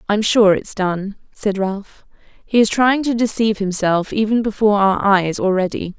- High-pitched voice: Yes, high, 205 Hz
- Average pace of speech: Yes, average, 180 wpm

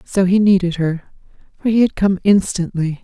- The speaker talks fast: No, average, 180 wpm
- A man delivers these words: No, female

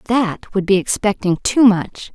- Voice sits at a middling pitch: No, high, 205 Hz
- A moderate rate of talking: Yes, average, 170 wpm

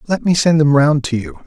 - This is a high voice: No, medium, 145 Hz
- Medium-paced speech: No, fast, 285 wpm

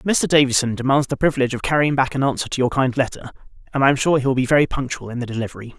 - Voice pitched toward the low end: Yes, low, 130 Hz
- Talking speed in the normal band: No, fast, 270 wpm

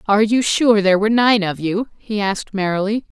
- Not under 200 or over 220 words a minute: Yes, fast, 205 wpm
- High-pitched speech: Yes, high, 210 Hz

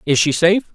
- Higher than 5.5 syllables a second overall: Yes, 6.4 syllables/s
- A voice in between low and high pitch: Yes, medium, 170 Hz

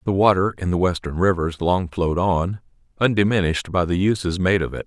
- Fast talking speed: No, average, 195 wpm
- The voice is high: No, very low, 90 Hz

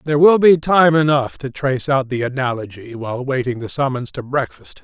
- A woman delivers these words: No, male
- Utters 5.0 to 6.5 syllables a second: Yes, 5.5 syllables/s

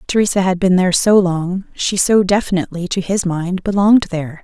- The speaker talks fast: No, average, 190 wpm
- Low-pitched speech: No, medium, 185 Hz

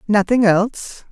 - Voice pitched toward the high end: Yes, high, 210 Hz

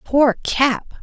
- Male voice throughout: No, female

